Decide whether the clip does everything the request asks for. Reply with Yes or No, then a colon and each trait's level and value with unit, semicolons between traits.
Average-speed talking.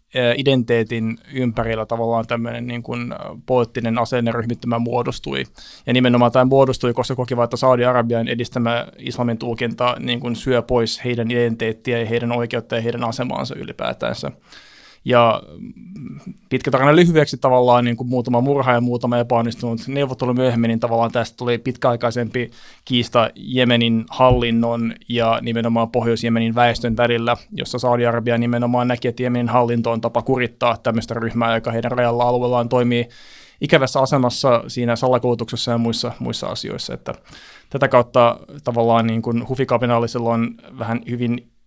Yes: average, 135 wpm